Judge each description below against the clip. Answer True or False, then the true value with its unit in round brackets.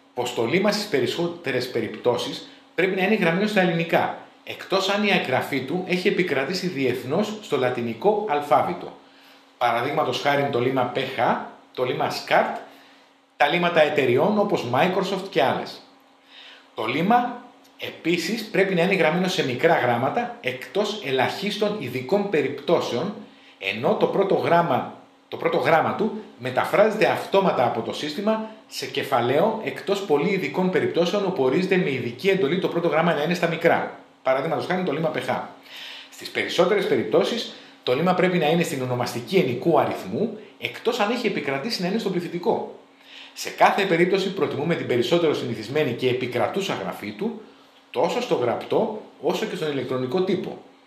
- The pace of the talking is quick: False (150 wpm)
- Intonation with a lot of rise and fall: True (6.4 semitones)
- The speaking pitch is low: False (175 Hz)